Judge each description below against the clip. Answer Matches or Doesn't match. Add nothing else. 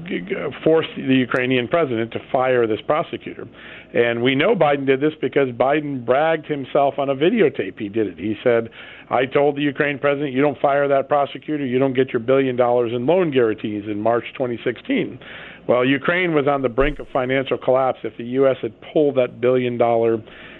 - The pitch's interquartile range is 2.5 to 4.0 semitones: Matches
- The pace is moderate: Matches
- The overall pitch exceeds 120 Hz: Matches